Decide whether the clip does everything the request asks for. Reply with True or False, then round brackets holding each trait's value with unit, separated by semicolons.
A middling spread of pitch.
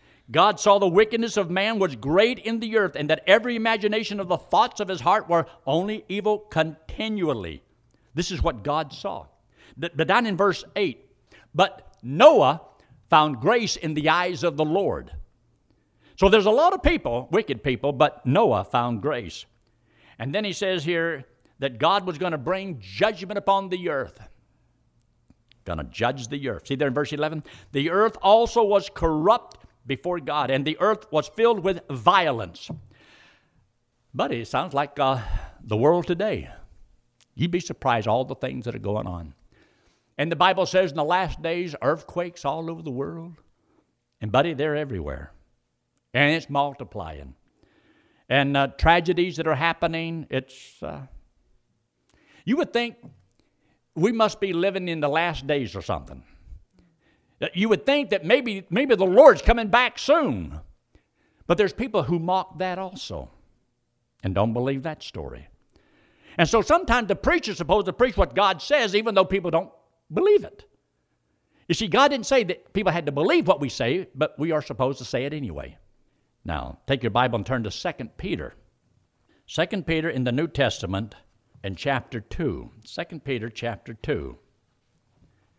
False (7.1 semitones)